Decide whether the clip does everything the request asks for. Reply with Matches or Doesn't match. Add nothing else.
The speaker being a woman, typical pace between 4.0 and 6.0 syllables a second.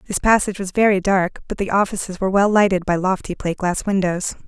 Doesn't match